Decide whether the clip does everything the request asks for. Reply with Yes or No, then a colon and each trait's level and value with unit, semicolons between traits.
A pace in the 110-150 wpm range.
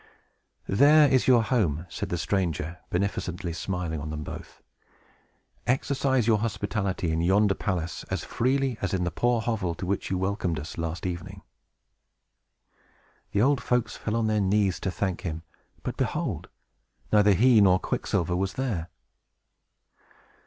Yes: average, 145 wpm